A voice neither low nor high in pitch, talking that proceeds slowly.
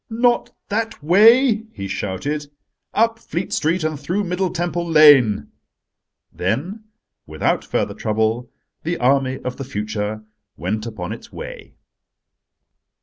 Yes: medium, 150 Hz; slow, 120 wpm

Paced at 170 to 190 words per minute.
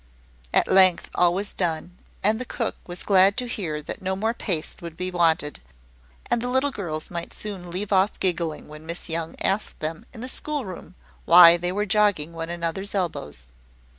Yes: average, 185 wpm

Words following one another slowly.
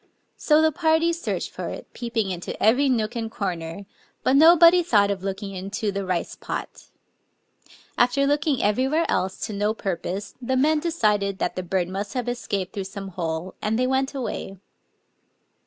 No: average, 170 wpm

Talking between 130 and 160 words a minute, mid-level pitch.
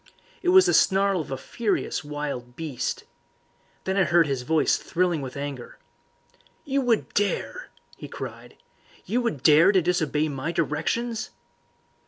Yes: average, 145 wpm; medium, 170 Hz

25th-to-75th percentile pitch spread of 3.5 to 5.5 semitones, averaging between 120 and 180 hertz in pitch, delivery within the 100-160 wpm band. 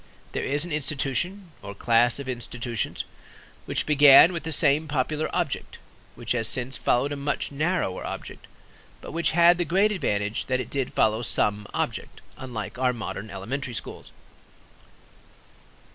Yes: average, 4.8 semitones; low, 135 Hz; average, 150 wpm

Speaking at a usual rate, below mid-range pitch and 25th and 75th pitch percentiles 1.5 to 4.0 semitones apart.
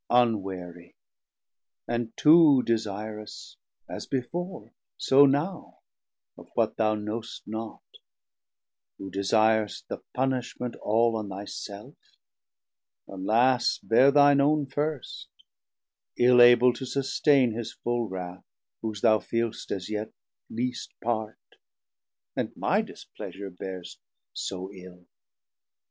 No: slow, 110 wpm; low, 115 Hz; average, 3.7 semitones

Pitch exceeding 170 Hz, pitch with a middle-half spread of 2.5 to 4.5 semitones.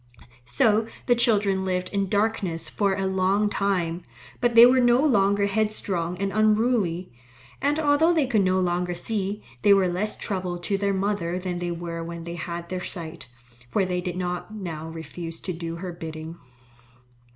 Yes: high, 190 Hz; average, 3.4 semitones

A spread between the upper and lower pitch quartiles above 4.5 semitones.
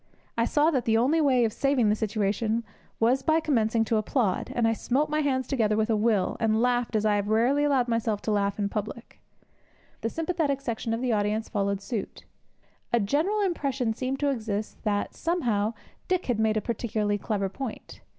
No: average, 4.0 semitones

